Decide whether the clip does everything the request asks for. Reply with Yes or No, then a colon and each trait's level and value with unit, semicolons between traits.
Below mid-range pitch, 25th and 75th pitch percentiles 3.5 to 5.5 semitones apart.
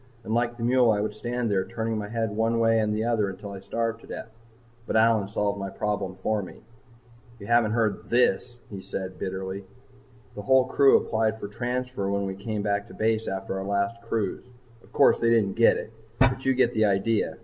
No: low, 110 Hz; narrow, 2.6 semitones